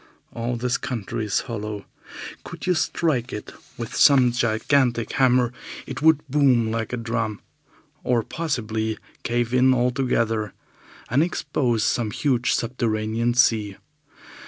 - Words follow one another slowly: Yes, slow, 125 wpm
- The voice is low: Yes, low, 120 Hz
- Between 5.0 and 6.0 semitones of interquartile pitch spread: No, narrow, 2.4 semitones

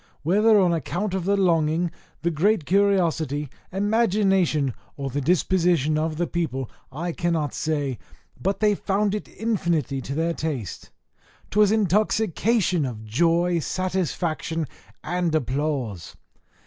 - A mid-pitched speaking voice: Yes, medium, 170 Hz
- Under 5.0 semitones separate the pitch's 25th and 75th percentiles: Yes, average, 4.3 semitones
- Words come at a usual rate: No, slow, 120 wpm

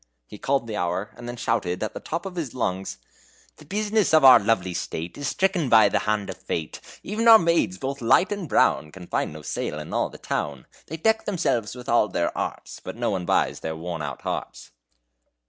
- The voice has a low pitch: Yes, low, 115 Hz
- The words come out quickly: Yes, fast, 215 wpm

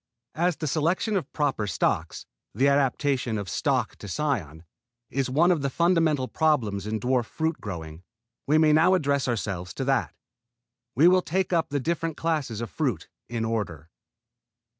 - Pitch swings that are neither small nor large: No, wide, 6.4 semitones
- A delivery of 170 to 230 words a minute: No, average, 160 wpm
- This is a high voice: No, medium, 140 Hz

